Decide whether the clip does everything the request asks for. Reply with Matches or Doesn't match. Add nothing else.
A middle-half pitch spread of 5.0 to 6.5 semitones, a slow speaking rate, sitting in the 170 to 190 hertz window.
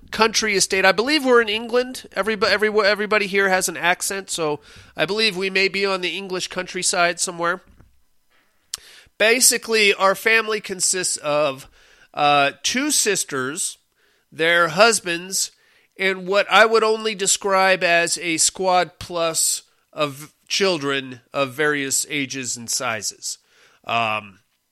Matches